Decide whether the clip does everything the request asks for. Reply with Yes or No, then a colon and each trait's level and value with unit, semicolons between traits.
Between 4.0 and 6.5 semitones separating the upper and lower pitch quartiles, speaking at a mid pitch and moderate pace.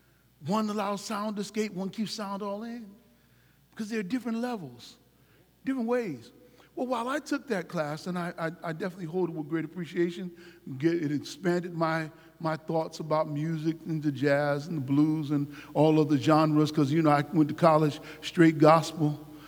Yes: average, 4.7 semitones; medium, 165 Hz; average, 190 wpm